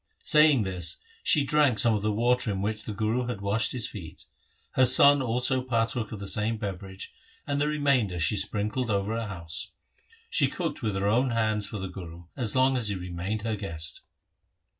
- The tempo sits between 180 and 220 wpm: Yes, average, 195 wpm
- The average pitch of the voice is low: Yes, low, 110 Hz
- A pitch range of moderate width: Yes, average, 4.0 semitones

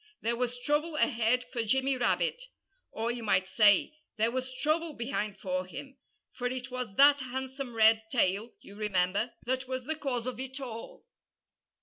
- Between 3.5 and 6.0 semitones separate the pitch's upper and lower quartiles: No, average, 3.1 semitones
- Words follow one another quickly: No, average, 165 wpm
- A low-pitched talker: No, high, 245 Hz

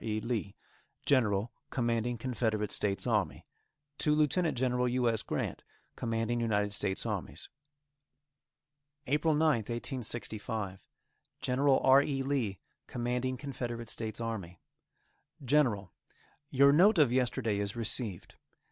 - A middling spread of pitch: Yes, average, 3.6 semitones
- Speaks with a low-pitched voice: Yes, low, 120 Hz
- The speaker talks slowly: Yes, slow, 110 wpm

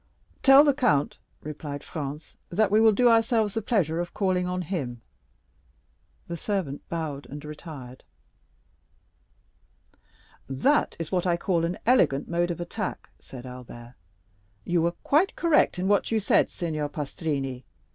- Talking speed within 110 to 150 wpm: Yes, average, 145 wpm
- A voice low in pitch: No, medium, 170 Hz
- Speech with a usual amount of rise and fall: No, wide, 6.1 semitones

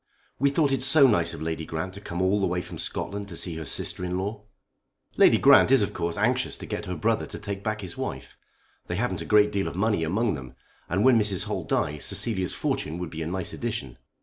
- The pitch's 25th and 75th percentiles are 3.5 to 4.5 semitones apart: Yes, average, 4.2 semitones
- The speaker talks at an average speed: No, fast, 240 wpm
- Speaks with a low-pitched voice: Yes, very low, 95 Hz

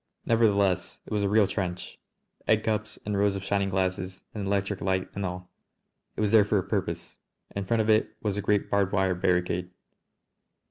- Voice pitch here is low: Yes, low, 100 Hz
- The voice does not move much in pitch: Yes, narrow, 1.9 semitones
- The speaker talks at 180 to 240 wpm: Yes, average, 190 wpm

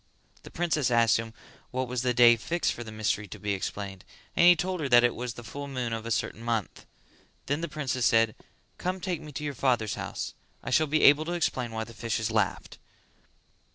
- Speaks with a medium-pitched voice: No, low, 120 Hz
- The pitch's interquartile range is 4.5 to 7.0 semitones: Yes, average, 4.9 semitones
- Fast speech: Yes, fast, 225 wpm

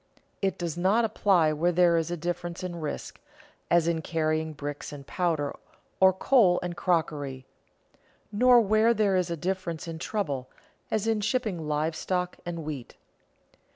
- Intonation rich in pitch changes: No, average, 3.4 semitones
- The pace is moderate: Yes, average, 155 wpm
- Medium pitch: Yes, medium, 175 Hz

